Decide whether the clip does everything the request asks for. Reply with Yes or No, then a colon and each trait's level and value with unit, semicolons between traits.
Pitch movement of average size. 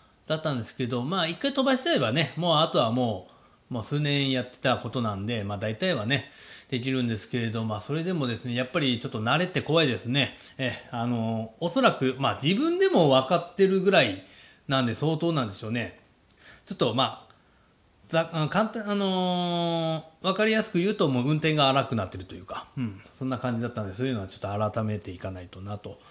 No: wide, 6.6 semitones